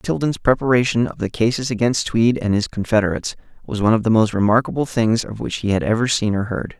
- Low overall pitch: Yes, low, 115 Hz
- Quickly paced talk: Yes, fast, 220 wpm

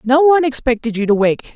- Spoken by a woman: No, male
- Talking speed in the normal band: No, fast, 230 wpm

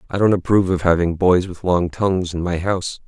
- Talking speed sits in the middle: No, fast, 235 wpm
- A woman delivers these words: No, male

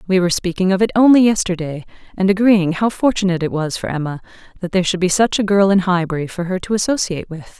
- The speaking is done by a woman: Yes, female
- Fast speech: Yes, fast, 230 wpm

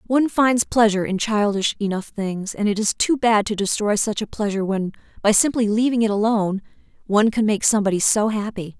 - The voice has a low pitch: No, high, 210 Hz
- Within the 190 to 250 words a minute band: Yes, average, 200 wpm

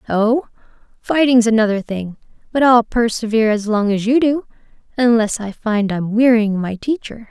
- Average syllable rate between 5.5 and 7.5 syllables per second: No, 4.9 syllables/s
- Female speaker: Yes, female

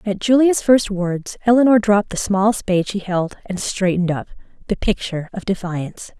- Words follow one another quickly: No, average, 175 wpm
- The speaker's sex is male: No, female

